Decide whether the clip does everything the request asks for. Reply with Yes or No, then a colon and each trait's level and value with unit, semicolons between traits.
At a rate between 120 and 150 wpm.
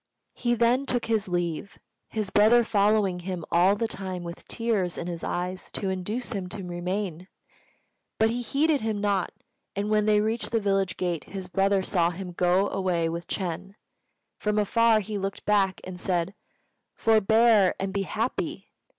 No: average, 170 wpm